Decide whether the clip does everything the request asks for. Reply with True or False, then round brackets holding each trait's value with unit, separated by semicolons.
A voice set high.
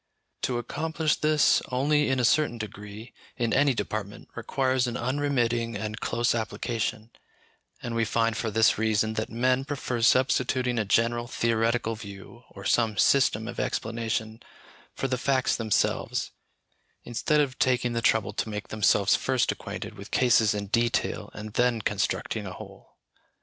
False (115 Hz)